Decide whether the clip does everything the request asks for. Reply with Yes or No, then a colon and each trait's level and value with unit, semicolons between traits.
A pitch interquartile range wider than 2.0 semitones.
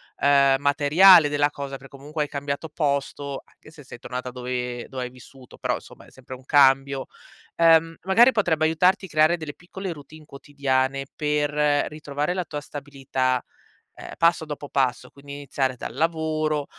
Yes: narrow, 2.6 semitones